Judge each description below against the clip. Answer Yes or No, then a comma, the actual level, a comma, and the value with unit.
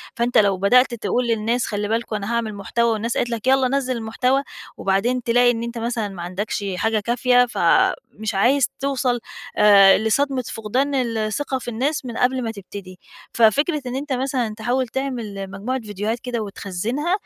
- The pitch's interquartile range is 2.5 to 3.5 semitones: Yes, average, 3.2 semitones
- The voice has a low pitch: No, high, 235 Hz